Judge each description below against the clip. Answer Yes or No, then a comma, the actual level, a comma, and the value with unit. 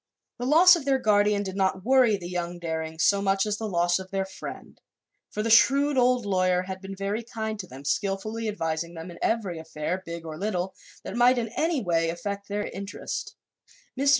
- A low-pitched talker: No, high, 195 Hz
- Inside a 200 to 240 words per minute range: Yes, fast, 205 wpm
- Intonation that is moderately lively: Yes, average, 4.3 semitones